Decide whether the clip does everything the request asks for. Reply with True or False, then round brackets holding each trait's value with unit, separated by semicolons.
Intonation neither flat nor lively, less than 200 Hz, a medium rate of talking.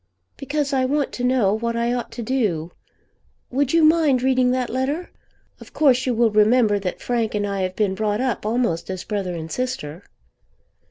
False (4.1 semitones; 240 Hz; 185 wpm)